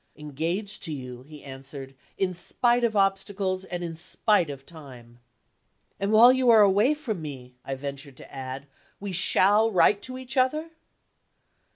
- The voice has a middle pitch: Yes, medium, 180 Hz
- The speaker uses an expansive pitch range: Yes, wide, 7.4 semitones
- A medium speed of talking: Yes, average, 160 wpm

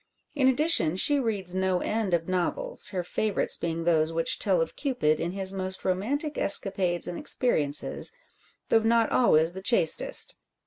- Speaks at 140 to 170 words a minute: Yes, average, 160 wpm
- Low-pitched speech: No, high, 190 Hz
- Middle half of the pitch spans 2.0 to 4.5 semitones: No, average, 4.9 semitones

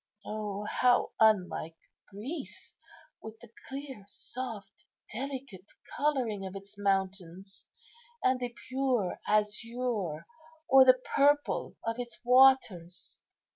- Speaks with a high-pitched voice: Yes, high, 220 Hz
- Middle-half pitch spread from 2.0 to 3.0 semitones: No, average, 4.7 semitones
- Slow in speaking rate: Yes, slow, 100 wpm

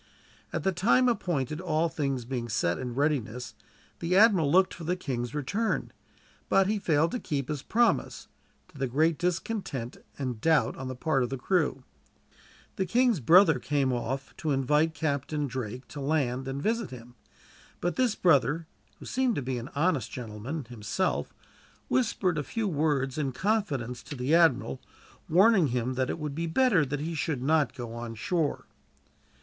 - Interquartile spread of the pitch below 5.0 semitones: No, average, 5.3 semitones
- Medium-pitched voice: Yes, medium, 145 Hz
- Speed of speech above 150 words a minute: Yes, average, 170 wpm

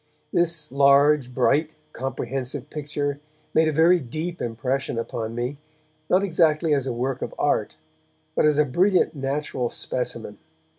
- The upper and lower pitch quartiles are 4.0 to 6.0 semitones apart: No, average, 3.6 semitones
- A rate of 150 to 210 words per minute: No, average, 140 wpm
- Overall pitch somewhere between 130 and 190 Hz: Yes, medium, 140 Hz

